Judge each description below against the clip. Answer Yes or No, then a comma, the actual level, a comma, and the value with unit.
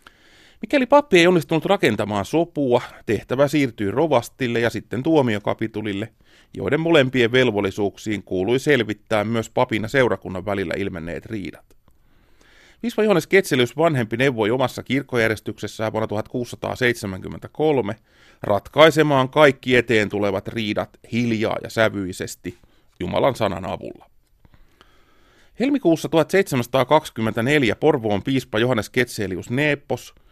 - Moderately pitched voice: No, low, 120 Hz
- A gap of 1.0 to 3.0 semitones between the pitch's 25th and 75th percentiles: No, wide, 5.4 semitones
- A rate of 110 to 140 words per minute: No, average, 100 wpm